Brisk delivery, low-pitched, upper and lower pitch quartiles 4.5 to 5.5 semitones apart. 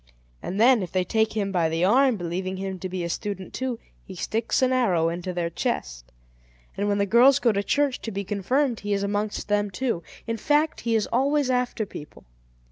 No: fast, 210 wpm; high, 205 Hz; average, 4.8 semitones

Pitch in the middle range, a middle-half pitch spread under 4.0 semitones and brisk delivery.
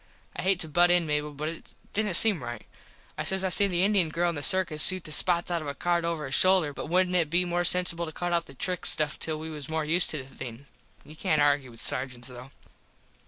Yes: medium, 165 Hz; average, 3.3 semitones; fast, 260 wpm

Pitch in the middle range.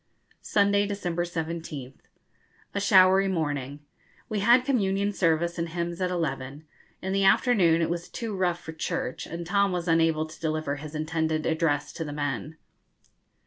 Yes: medium, 170 Hz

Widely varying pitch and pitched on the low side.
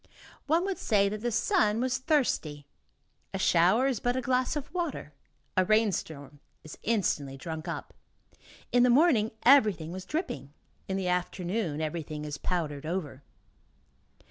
No: wide, 7.9 semitones; high, 195 Hz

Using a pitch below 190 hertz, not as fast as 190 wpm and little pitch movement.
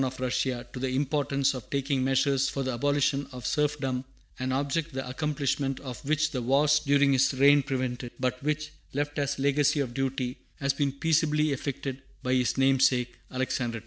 Yes: low, 135 Hz; average, 180 wpm; narrow, 1.9 semitones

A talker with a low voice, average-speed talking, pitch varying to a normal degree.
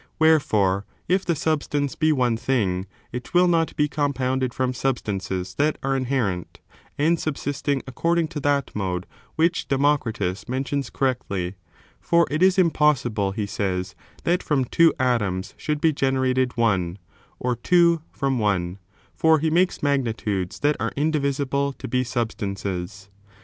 No: low, 130 Hz; average, 145 wpm; wide, 6.3 semitones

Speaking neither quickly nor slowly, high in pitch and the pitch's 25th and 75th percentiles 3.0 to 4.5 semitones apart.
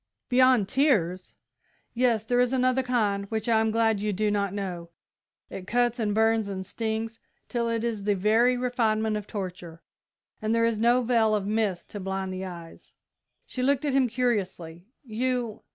Yes: average, 175 wpm; high, 220 Hz; average, 3.4 semitones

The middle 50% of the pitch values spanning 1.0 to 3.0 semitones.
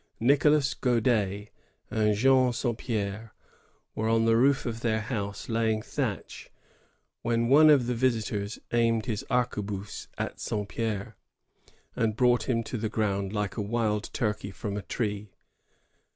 Yes: narrow, 2.6 semitones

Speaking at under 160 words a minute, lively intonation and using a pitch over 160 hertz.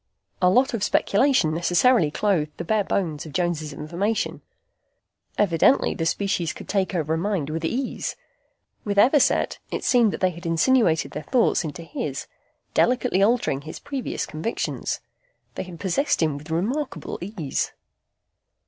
Yes: average, 150 wpm; wide, 5.9 semitones; medium, 185 Hz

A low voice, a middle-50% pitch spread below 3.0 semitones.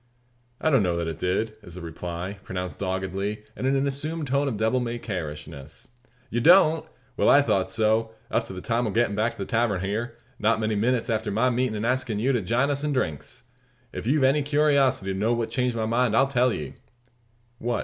No: low, 115 Hz; average, 4.8 semitones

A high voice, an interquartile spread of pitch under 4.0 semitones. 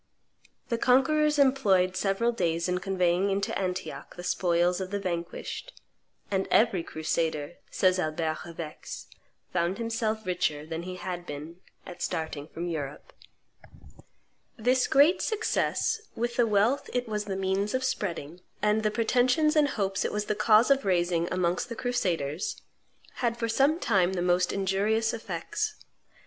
No: high, 195 Hz; average, 5.0 semitones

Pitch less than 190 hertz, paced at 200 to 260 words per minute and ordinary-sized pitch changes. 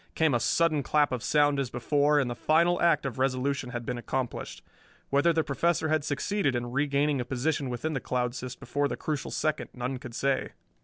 Yes: medium, 140 Hz; fast, 205 wpm; average, 3.3 semitones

